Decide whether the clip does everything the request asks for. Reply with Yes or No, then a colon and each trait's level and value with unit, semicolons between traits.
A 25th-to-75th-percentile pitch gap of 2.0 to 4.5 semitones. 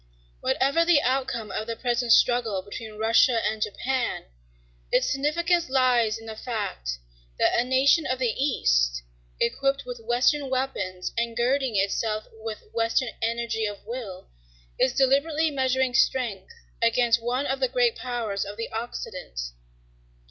Yes: average, 3.3 semitones